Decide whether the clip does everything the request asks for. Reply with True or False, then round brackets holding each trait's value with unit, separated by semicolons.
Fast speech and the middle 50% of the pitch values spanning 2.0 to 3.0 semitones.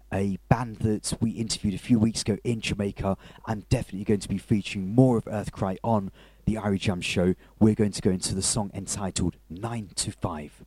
True (210 wpm; 2.7 semitones)